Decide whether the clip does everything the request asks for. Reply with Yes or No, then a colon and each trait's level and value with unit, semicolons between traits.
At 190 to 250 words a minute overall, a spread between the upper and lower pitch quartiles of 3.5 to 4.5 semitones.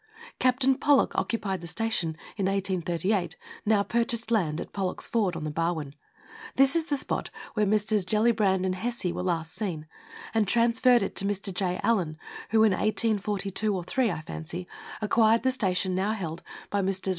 No: average, 170 wpm; average, 3.8 semitones